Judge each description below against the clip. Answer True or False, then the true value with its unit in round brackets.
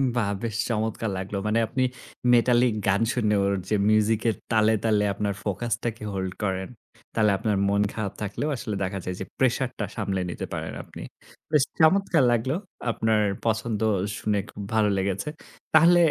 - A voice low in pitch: True (110 Hz)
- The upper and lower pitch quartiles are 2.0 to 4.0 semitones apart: True (2.8 semitones)